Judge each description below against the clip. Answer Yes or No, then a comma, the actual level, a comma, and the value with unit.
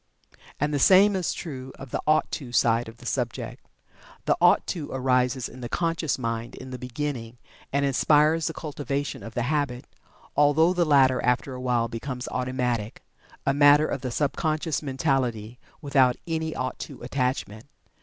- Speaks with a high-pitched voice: No, low, 130 Hz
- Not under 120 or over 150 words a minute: No, average, 170 wpm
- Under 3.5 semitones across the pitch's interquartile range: Yes, average, 3.1 semitones